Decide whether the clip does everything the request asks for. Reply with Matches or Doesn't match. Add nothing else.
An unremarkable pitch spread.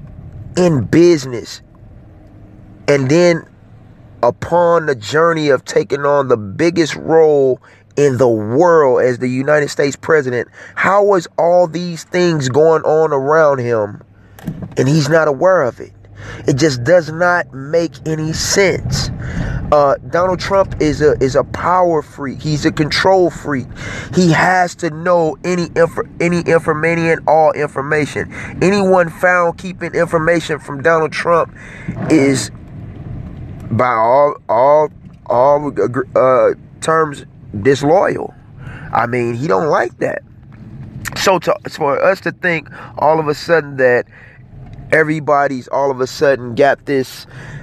Matches